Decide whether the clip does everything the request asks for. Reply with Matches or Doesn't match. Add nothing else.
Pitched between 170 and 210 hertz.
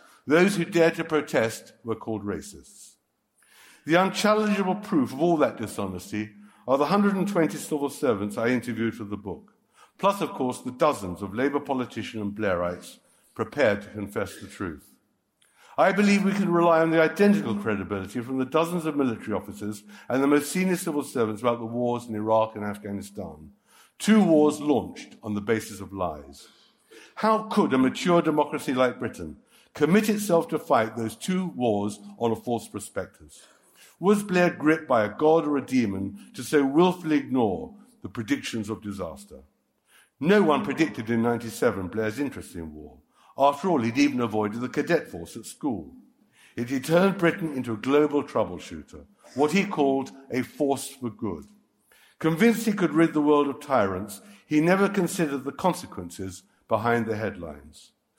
Doesn't match